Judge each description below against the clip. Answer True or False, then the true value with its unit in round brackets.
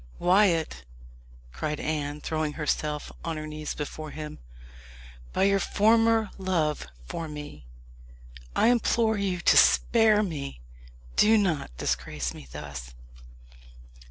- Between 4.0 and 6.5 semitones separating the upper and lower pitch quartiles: True (5.2 semitones)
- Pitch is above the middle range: False (155 Hz)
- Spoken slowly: True (115 wpm)